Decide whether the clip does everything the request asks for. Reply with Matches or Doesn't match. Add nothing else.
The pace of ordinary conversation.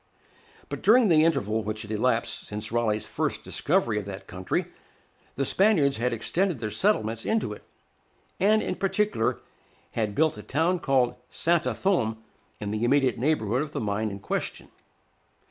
Matches